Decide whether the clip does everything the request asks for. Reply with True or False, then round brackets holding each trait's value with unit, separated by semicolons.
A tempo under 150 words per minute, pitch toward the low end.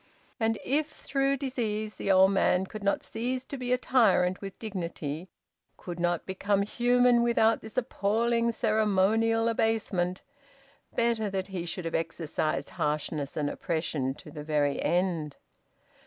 False (140 wpm; 200 Hz)